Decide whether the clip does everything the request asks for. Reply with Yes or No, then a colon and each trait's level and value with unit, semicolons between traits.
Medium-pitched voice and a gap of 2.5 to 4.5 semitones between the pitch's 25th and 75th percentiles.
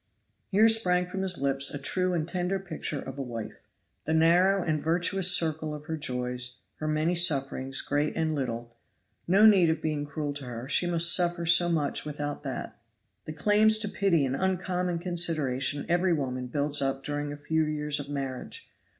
Yes: medium, 155 Hz; average, 3.9 semitones